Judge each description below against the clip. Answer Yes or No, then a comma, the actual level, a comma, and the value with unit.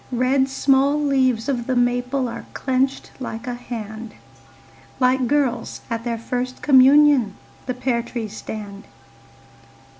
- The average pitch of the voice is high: Yes, very high, 250 Hz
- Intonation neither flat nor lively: No, narrow, 2.3 semitones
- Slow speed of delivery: Yes, slow, 125 wpm